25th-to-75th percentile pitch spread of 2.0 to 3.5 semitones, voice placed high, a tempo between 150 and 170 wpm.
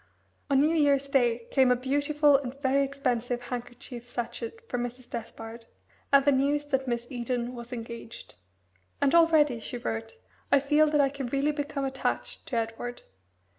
Yes: average, 2.8 semitones; very high, 265 Hz; average, 165 wpm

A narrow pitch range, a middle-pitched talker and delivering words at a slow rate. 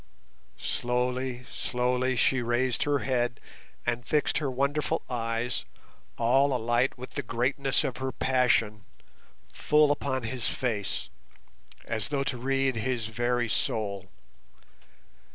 No: narrow, 2.0 semitones; low, 125 Hz; slow, 115 wpm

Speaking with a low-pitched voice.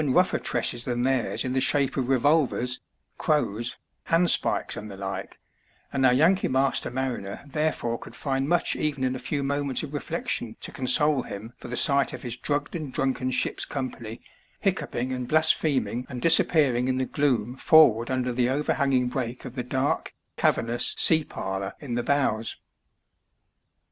Yes: low, 130 Hz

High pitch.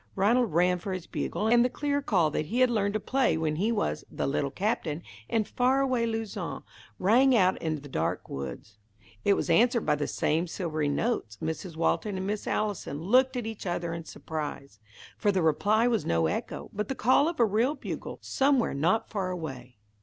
Yes: high, 200 Hz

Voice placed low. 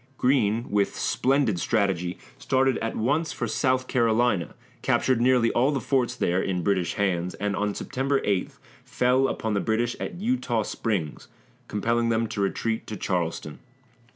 Yes: low, 115 Hz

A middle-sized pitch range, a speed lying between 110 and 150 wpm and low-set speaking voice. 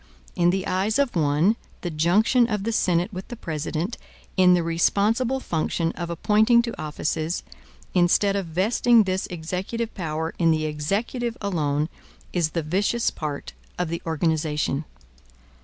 No: average, 4.8 semitones; average, 145 wpm; medium, 180 Hz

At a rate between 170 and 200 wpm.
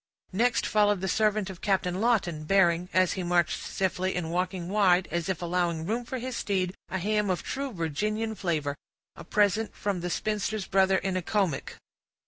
Yes: average, 175 wpm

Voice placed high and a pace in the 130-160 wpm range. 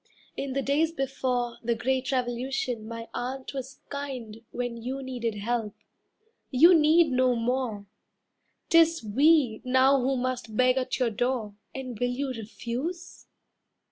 Yes: very high, 255 Hz; average, 140 wpm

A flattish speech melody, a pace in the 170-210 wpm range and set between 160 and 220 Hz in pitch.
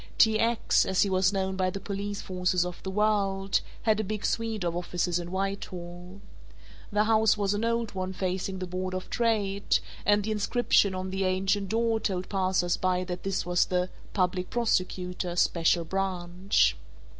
Yes: narrow, 2.1 semitones; average, 175 wpm; high, 190 Hz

